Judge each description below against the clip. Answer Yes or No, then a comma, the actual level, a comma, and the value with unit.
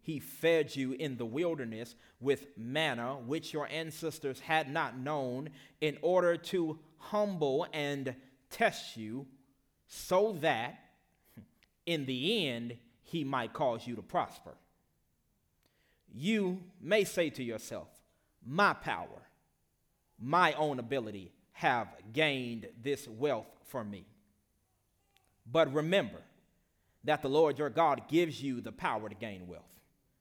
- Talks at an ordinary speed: No, slow, 125 wpm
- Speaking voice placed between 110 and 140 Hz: Yes, low, 135 Hz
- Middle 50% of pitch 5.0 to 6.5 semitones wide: Yes, wide, 5.5 semitones